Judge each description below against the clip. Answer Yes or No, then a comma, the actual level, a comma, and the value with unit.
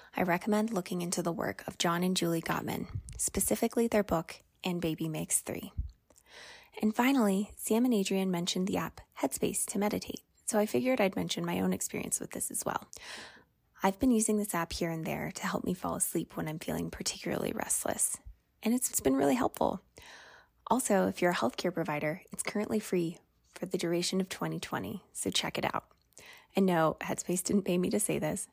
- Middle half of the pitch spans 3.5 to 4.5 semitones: Yes, average, 3.8 semitones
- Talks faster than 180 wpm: Yes, average, 190 wpm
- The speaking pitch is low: No, medium, 185 Hz